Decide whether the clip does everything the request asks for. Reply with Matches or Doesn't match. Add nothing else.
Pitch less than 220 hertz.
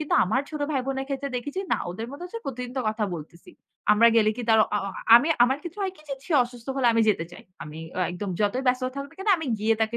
Doesn't match